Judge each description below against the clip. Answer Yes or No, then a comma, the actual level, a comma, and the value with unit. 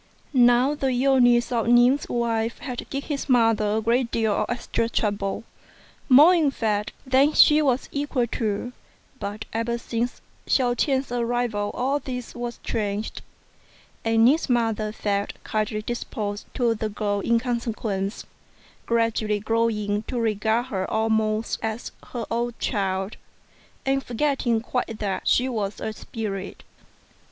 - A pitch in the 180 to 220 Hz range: No, high, 230 Hz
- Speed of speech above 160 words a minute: No, average, 140 wpm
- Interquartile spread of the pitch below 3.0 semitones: Yes, narrow, 2.5 semitones